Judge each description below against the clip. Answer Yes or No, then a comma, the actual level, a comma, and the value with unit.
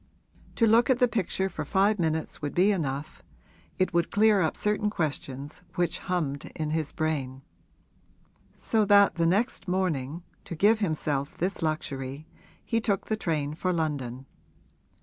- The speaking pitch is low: No, medium, 170 Hz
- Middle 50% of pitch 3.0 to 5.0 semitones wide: No, wide, 5.4 semitones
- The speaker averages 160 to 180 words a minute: No, average, 150 wpm